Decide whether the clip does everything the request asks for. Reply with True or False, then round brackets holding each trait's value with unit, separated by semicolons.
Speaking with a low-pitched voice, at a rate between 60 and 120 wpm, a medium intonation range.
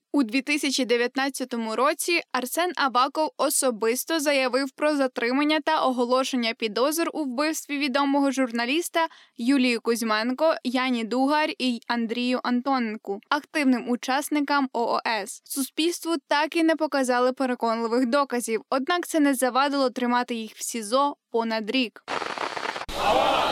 False (265 Hz; 110 wpm; 3.4 semitones)